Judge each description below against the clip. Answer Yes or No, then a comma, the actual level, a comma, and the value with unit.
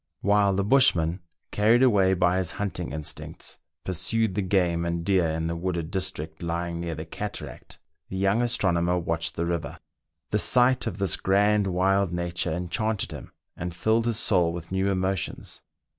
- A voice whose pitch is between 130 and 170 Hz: No, very low, 95 Hz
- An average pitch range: Yes, average, 3.0 semitones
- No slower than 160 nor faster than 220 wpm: Yes, average, 165 wpm